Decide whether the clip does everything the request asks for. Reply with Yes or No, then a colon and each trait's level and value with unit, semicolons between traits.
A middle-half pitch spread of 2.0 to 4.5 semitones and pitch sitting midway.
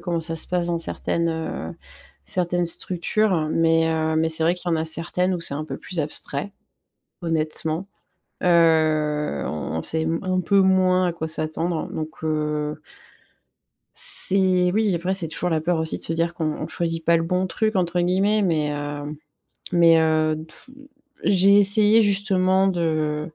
Yes: narrow, 2.6 semitones; medium, 165 Hz